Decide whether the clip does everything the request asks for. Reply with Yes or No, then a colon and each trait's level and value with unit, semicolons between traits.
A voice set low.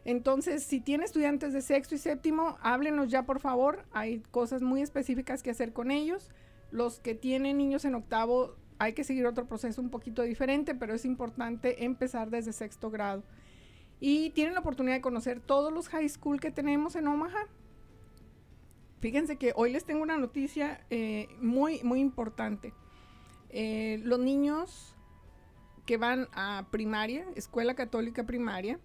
No: very high, 255 Hz